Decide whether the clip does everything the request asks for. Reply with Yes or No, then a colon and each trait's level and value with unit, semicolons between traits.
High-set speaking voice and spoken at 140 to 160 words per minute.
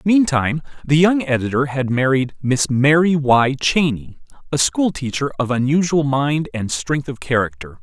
No: medium, 140 Hz; average, 145 wpm